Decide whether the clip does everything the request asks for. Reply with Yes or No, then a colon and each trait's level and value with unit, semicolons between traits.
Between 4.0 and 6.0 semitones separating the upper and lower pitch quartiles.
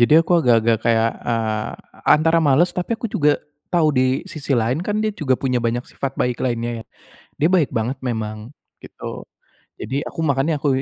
Yes: average, 4.9 semitones